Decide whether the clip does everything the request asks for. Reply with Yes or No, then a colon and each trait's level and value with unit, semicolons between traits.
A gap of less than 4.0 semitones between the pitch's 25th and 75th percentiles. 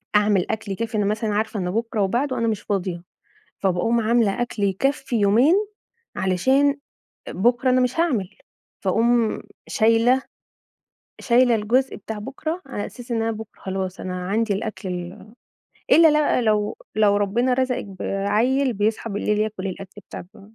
Yes: average, 3.4 semitones